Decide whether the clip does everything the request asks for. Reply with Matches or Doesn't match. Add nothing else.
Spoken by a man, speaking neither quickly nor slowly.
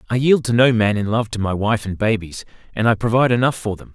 Doesn't match